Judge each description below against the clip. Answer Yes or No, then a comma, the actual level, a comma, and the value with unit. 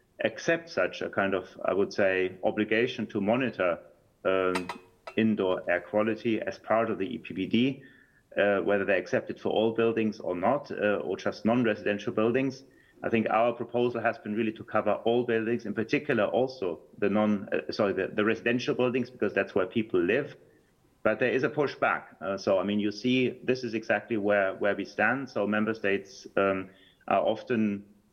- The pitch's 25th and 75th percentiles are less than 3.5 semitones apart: Yes, narrow, 2.5 semitones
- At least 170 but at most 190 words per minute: Yes, average, 185 wpm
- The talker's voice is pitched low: Yes, low, 110 Hz